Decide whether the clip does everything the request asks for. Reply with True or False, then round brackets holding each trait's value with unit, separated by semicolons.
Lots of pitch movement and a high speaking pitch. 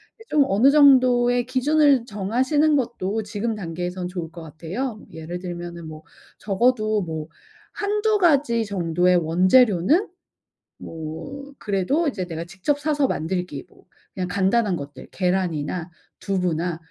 True (6.8 semitones; 195 Hz)